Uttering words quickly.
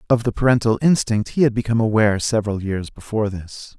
No: average, 190 wpm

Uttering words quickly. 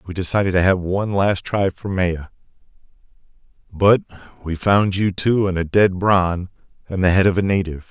No: average, 180 wpm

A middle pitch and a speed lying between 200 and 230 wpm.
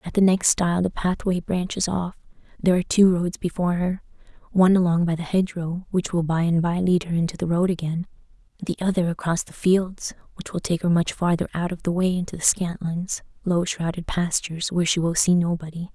Yes: medium, 175 Hz; fast, 205 wpm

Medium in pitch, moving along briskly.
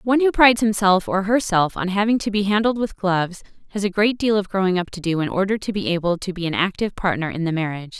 No: high, 195 Hz; fast, 265 wpm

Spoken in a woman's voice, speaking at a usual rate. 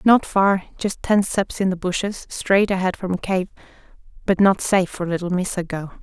Yes: female; average, 190 wpm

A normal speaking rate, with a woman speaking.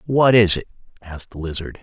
No: average, 195 wpm; male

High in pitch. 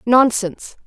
Yes: high, 230 Hz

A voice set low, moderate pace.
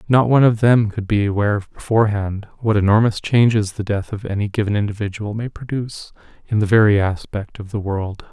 Yes: low, 105 Hz; average, 190 wpm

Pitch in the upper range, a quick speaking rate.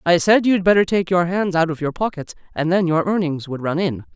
No: medium, 170 Hz; fast, 260 wpm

